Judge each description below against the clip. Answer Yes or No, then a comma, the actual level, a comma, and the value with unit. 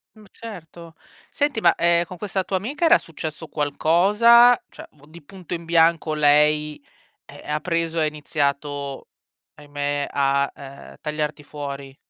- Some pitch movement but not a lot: Yes, average, 3.2 semitones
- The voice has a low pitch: No, medium, 155 Hz